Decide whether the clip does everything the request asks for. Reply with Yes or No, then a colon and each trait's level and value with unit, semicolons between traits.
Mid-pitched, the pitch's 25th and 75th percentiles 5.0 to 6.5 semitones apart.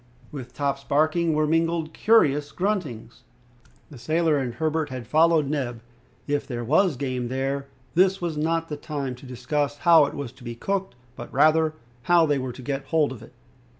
No: medium, 145 Hz; average, 3.8 semitones